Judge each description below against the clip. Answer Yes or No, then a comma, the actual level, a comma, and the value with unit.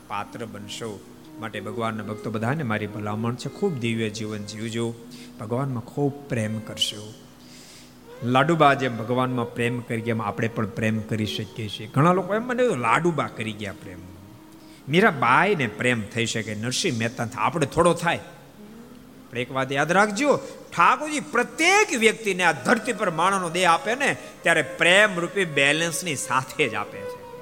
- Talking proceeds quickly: Yes, fast, 150 wpm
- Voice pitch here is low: Yes, low, 125 Hz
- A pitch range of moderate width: No, wide, 8.1 semitones